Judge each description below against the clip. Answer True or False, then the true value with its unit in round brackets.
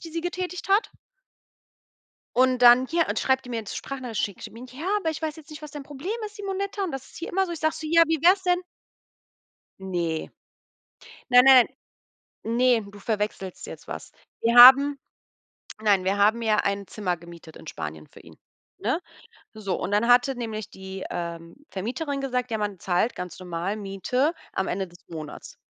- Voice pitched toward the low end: False (240 Hz)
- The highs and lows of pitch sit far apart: True (7.5 semitones)